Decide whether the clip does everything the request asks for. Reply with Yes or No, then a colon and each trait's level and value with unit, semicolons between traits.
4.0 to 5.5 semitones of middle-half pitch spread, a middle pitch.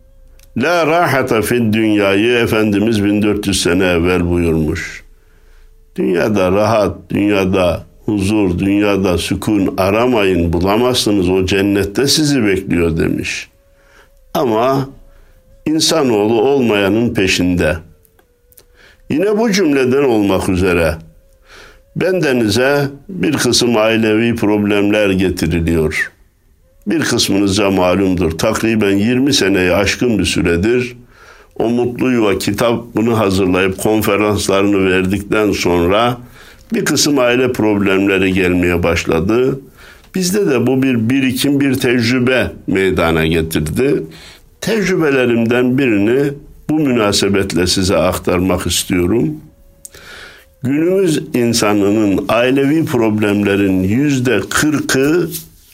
No: average, 5.2 semitones; low, 100 Hz